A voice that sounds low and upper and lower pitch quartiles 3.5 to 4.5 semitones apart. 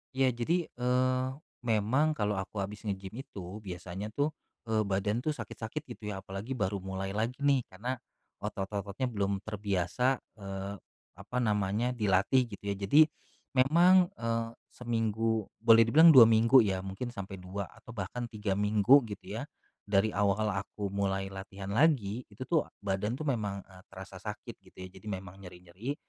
Yes: low, 105 Hz; average, 3.8 semitones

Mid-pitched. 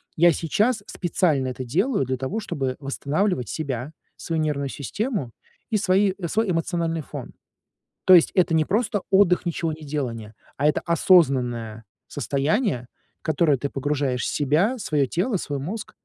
Yes: medium, 155 Hz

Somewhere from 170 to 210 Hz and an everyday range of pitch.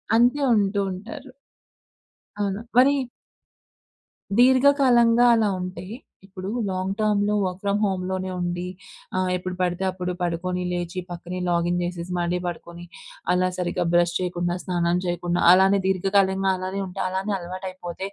No: medium, 185 Hz; narrow, 2.1 semitones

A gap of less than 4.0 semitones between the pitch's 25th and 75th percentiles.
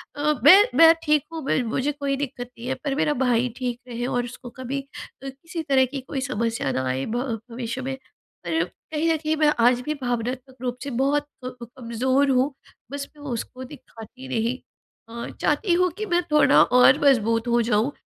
Yes: average, 3.3 semitones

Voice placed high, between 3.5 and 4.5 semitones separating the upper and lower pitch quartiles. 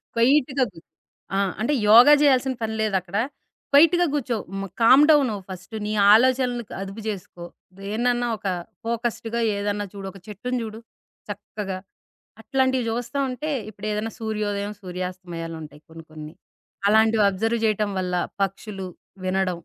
Yes: high, 215 Hz; average, 3.9 semitones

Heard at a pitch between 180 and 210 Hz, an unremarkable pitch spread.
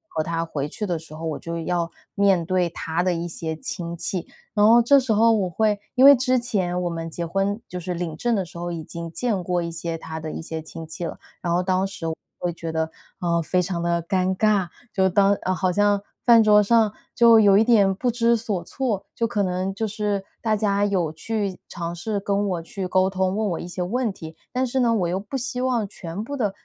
Yes: high, 190 Hz; average, 4.1 semitones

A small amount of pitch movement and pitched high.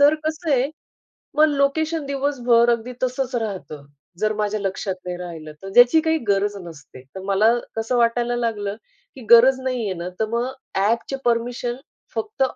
No: average, 4.4 semitones; high, 235 Hz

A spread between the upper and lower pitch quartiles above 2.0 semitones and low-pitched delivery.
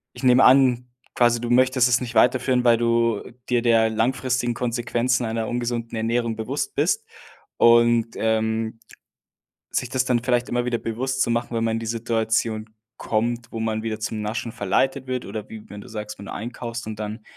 No: narrow, 1.7 semitones; low, 115 Hz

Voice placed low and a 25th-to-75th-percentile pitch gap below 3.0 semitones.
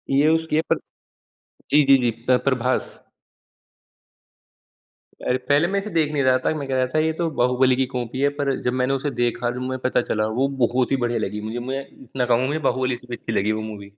Yes: low, 130 Hz; narrow, 2.4 semitones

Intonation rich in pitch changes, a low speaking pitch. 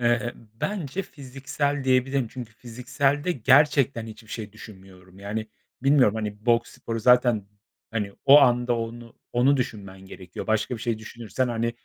No: average, 3.4 semitones; low, 120 Hz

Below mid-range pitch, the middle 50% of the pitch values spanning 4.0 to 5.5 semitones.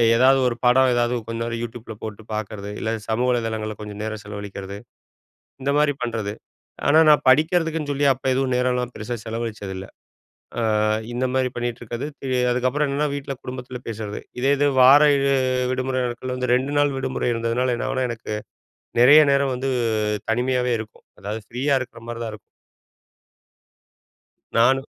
No: low, 125 Hz; average, 2.9 semitones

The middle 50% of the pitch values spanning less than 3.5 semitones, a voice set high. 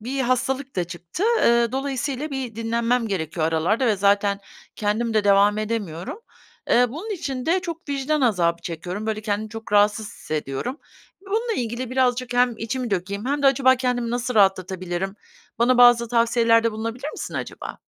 No: average, 4.1 semitones; high, 230 Hz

